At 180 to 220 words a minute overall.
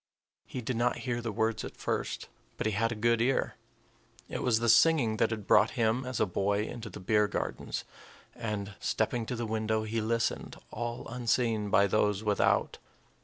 Yes: average, 185 wpm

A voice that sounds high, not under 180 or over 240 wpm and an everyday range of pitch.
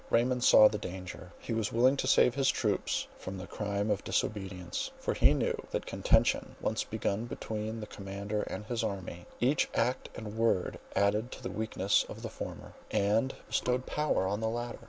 No: low, 110 Hz; average, 185 wpm; average, 3.1 semitones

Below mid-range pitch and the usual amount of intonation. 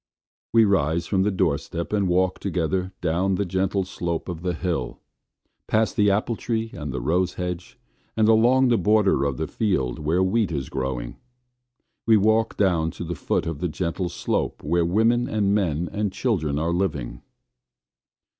Yes: very low, 90 Hz; average, 4.3 semitones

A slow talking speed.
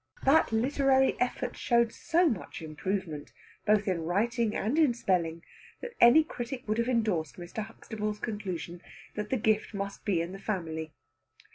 No: average, 155 wpm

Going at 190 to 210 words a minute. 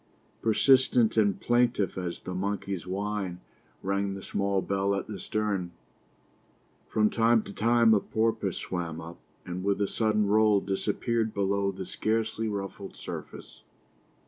No: average, 140 wpm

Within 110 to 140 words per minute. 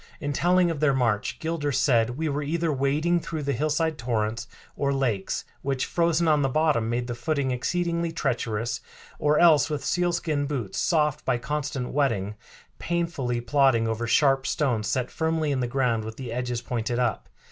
No: average, 175 wpm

